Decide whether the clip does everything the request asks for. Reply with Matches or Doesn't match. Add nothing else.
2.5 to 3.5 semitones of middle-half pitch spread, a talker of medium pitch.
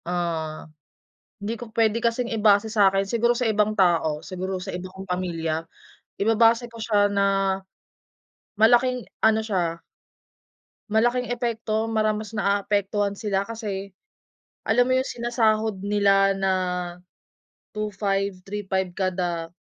Doesn't match